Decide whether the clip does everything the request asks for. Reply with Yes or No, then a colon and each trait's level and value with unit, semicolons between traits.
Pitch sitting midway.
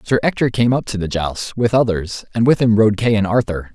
No: low, 110 Hz